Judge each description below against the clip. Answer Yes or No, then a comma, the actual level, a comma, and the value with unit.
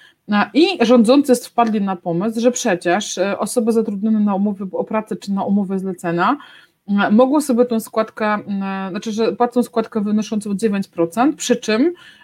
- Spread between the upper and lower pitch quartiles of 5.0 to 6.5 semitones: No, average, 3.6 semitones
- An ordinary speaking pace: Yes, average, 140 wpm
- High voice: Yes, high, 220 Hz